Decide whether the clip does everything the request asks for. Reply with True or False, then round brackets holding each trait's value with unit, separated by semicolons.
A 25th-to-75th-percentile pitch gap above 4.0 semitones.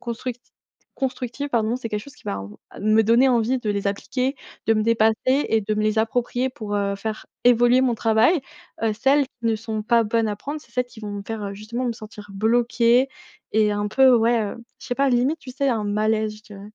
False (2.7 semitones)